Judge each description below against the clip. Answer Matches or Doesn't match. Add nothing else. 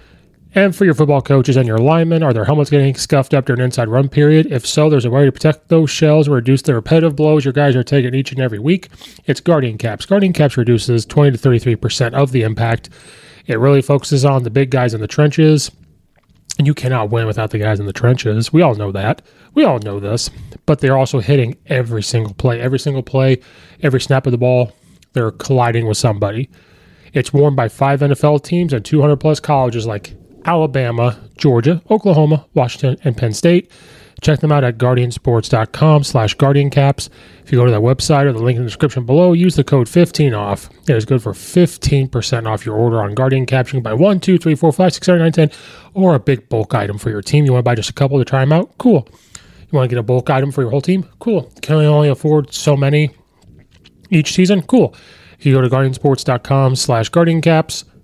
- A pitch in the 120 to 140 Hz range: Matches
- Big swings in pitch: Doesn't match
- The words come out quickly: Matches